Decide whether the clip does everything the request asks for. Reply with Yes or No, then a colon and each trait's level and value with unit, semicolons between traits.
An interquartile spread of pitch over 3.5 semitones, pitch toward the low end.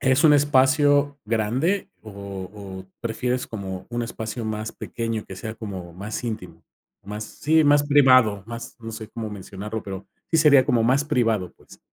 Yes: average, 4.1 semitones; low, 115 Hz